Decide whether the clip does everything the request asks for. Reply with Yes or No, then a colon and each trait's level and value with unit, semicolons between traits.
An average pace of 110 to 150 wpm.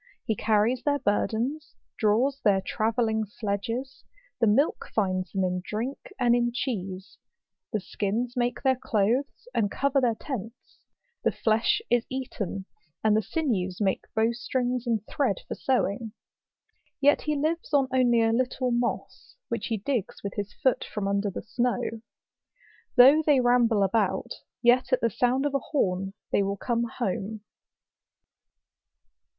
Yes: average, 145 wpm